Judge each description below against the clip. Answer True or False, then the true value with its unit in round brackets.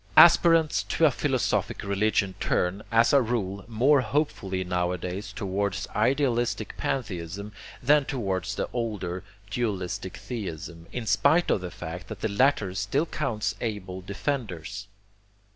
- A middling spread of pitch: True (5.0 semitones)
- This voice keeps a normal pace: False (125 wpm)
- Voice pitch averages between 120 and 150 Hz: False (105 Hz)